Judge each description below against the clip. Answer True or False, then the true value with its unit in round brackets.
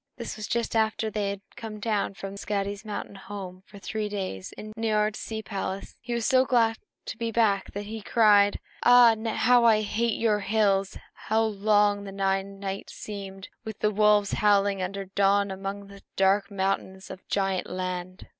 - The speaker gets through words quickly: False (185 wpm)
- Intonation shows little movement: True (1.9 semitones)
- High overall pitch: True (205 Hz)